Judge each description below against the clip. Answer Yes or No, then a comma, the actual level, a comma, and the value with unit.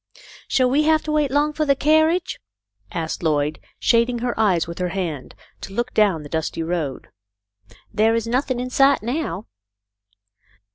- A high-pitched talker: Yes, high, 230 Hz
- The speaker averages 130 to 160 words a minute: No, average, 175 wpm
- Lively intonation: Yes, wide, 8.8 semitones